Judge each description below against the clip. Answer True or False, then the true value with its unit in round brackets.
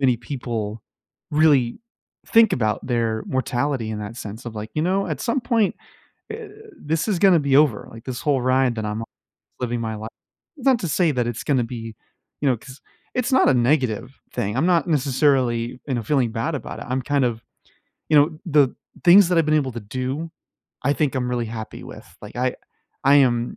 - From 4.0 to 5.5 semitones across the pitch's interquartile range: True (4.6 semitones)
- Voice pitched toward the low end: True (130 Hz)